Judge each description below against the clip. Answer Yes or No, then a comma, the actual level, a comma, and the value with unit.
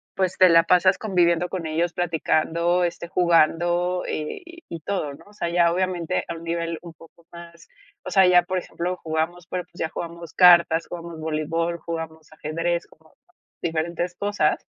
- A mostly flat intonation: Yes, narrow, 1.5 semitones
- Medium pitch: Yes, medium, 170 Hz